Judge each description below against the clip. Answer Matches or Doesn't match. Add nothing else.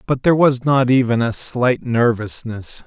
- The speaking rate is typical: Matches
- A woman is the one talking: Doesn't match